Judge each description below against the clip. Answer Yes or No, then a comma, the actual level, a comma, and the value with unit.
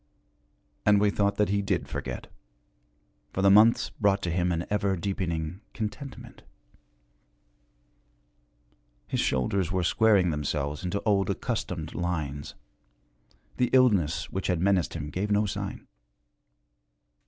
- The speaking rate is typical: No, slow, 120 wpm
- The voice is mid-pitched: No, very low, 95 Hz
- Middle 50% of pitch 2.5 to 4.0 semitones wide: Yes, average, 3.3 semitones